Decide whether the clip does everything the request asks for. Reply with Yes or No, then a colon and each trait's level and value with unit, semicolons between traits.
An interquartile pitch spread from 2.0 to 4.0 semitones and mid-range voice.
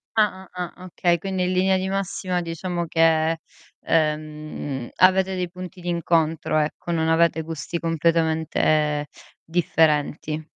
Yes: narrow, 2.5 semitones; medium, 165 Hz